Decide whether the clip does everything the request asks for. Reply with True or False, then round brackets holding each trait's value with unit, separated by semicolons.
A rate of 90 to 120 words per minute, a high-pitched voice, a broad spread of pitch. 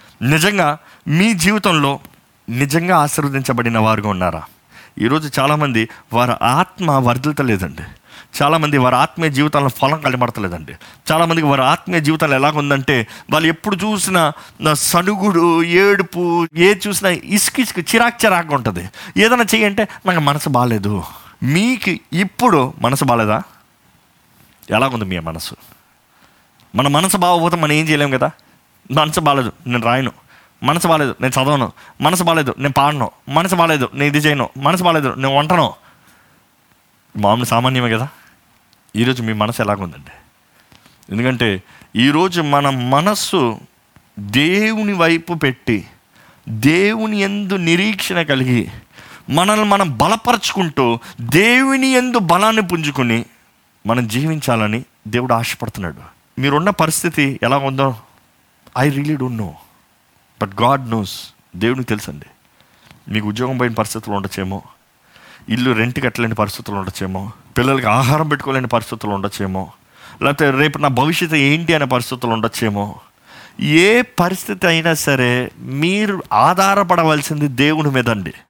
False (115 wpm; 140 Hz; 6.4 semitones)